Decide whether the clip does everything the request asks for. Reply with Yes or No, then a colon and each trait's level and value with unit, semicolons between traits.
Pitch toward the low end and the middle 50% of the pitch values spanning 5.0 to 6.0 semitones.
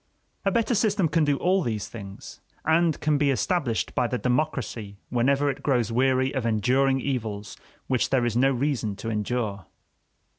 No: low, 130 Hz; average, 4.3 semitones